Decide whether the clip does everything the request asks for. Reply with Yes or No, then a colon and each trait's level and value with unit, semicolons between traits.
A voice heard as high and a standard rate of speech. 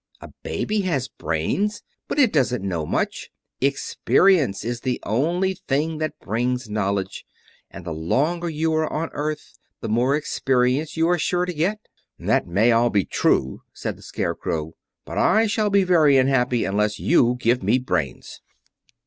No: low, 135 Hz; average, 160 wpm